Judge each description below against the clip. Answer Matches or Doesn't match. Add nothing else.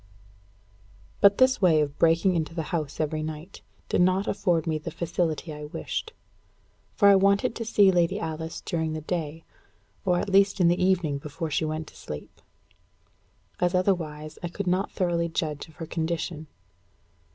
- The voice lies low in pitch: Doesn't match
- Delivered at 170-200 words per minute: Matches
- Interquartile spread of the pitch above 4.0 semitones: Doesn't match